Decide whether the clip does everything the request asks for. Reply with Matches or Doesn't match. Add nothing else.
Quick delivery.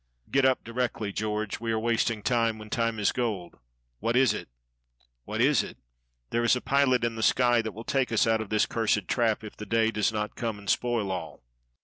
Matches